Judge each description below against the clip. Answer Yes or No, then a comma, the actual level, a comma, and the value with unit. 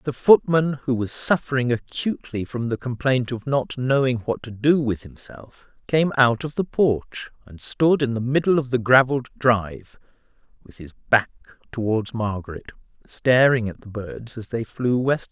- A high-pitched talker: No, low, 125 Hz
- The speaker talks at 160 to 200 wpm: Yes, average, 170 wpm